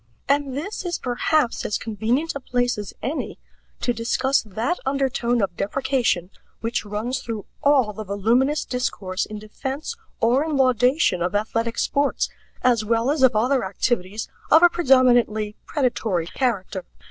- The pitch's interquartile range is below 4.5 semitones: Yes, average, 4.1 semitones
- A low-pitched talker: No, high, 245 Hz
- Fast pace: No, average, 145 wpm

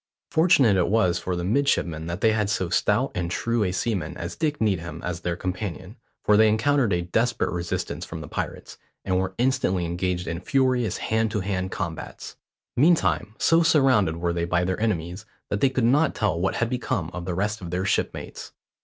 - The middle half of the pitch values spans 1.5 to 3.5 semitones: No, average, 4.8 semitones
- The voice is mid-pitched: No, very low, 95 Hz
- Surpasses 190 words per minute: Yes, average, 200 wpm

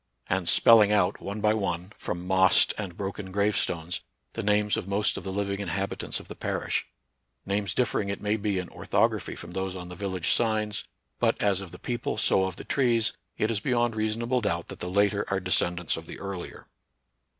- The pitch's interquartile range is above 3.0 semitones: No, narrow, 2.4 semitones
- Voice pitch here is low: Yes, low, 100 Hz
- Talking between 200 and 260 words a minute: Yes, fast, 205 wpm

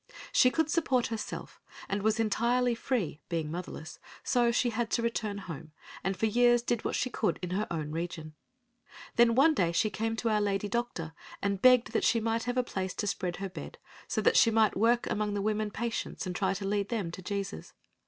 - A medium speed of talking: No, fast, 210 wpm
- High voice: Yes, high, 215 Hz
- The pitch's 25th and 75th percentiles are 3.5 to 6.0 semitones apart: Yes, average, 3.8 semitones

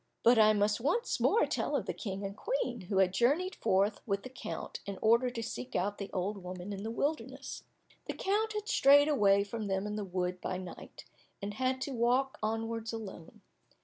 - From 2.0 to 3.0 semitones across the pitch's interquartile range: No, average, 4.7 semitones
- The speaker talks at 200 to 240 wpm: Yes, fast, 205 wpm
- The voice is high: Yes, high, 215 Hz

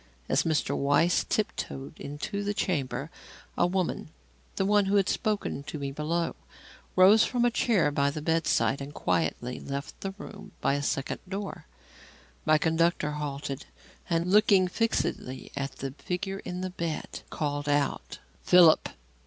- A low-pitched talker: No, medium, 165 Hz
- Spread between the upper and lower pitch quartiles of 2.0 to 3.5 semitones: No, average, 5.2 semitones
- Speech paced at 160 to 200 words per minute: No, average, 150 wpm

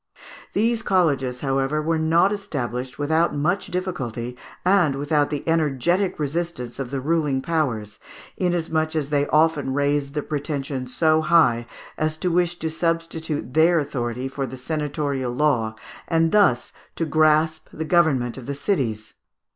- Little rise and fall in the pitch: No, average, 3.6 semitones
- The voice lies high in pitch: No, medium, 150 Hz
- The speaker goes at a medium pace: Yes, average, 145 wpm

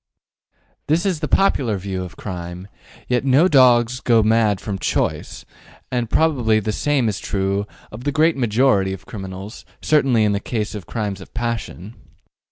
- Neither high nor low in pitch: No, low, 110 Hz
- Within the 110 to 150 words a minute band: No, average, 165 wpm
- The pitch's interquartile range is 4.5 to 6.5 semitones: Yes, average, 4.8 semitones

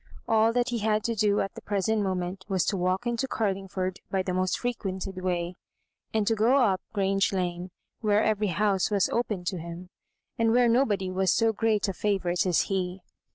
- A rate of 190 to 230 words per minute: Yes, average, 200 wpm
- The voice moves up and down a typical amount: Yes, average, 3.0 semitones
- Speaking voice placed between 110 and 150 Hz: No, high, 195 Hz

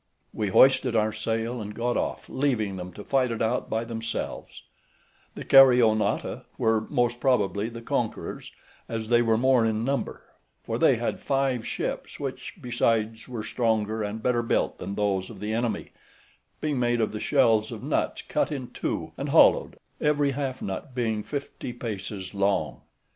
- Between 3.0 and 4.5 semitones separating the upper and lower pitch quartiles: No, narrow, 2.6 semitones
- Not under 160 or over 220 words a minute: Yes, average, 165 wpm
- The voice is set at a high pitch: No, low, 115 Hz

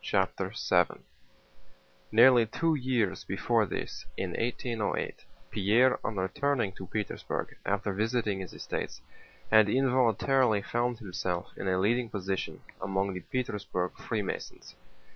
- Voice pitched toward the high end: No, low, 105 Hz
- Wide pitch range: No, average, 4.0 semitones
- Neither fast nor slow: No, slow, 120 wpm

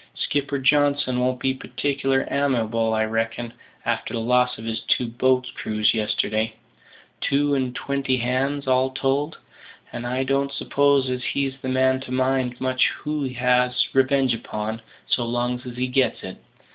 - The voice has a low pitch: Yes, low, 130 Hz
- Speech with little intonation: Yes, narrow, 2.0 semitones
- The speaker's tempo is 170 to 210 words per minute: No, average, 160 wpm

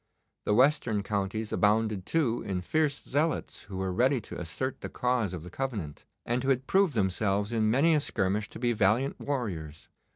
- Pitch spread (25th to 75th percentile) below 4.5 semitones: No, wide, 5.4 semitones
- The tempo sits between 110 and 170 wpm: No, average, 185 wpm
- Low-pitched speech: Yes, low, 110 Hz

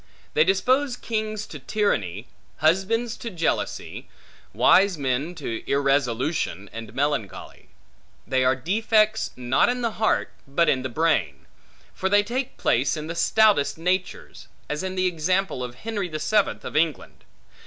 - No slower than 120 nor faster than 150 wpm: Yes, average, 145 wpm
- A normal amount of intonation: No, wide, 7.7 semitones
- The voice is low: No, medium, 165 Hz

